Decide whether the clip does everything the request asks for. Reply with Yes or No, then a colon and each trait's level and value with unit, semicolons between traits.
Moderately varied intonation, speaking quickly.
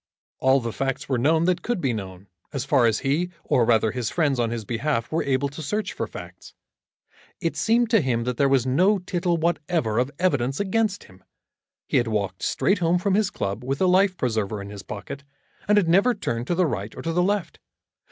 No: wide, 7.5 semitones; fast, 220 wpm